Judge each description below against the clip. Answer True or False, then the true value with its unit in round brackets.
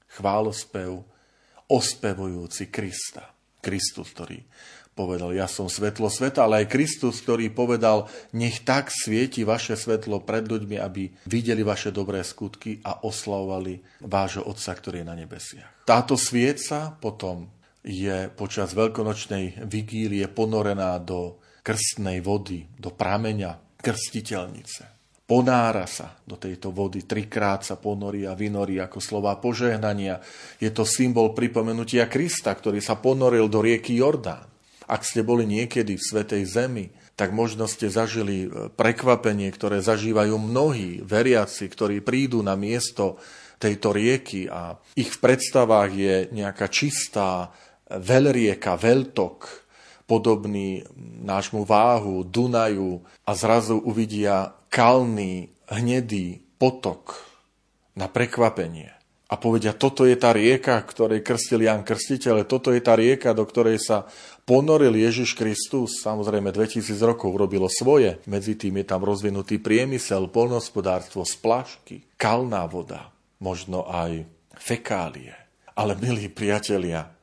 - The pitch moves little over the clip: False (3.1 semitones)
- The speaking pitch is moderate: False (105 Hz)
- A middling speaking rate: True (120 wpm)